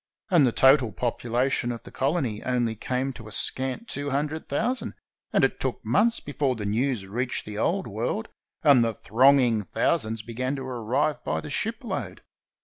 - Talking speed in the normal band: Yes, average, 175 wpm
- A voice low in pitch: Yes, low, 125 Hz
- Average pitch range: Yes, average, 3.9 semitones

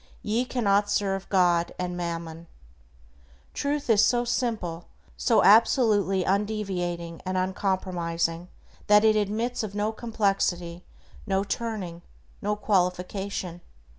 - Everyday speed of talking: No, slow, 105 wpm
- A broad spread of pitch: No, average, 3.4 semitones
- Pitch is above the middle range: Yes, high, 195 Hz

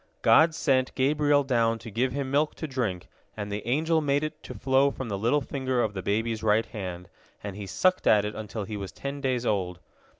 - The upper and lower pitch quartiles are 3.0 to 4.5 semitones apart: No, average, 5.1 semitones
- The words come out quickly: Yes, fast, 220 wpm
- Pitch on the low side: Yes, low, 120 Hz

